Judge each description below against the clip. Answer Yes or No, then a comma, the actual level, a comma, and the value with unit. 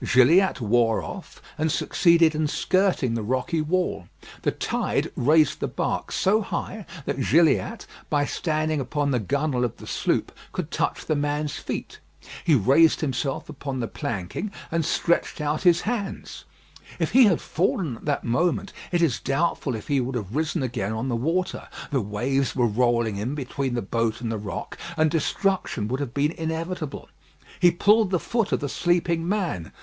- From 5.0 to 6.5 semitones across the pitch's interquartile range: Yes, wide, 5.5 semitones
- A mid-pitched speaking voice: Yes, medium, 145 Hz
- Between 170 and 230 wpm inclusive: Yes, average, 175 wpm